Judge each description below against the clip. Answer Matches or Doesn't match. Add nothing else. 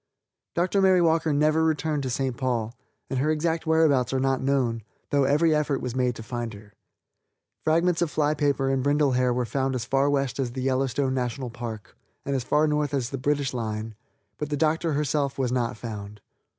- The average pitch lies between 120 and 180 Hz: Matches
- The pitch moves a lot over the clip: Doesn't match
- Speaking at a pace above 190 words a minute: Matches